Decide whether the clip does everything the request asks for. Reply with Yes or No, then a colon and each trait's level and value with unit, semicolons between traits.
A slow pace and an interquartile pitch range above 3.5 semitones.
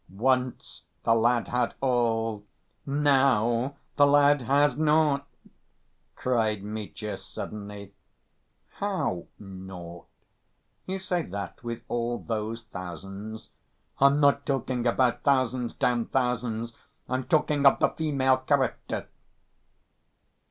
Yes: slow, 100 wpm; average, 4.2 semitones